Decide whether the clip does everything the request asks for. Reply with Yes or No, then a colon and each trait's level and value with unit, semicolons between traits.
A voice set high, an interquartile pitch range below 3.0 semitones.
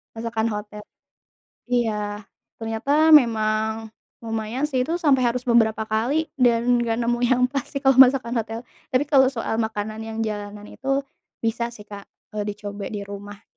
Yes: high, 225 Hz; narrow, 2.6 semitones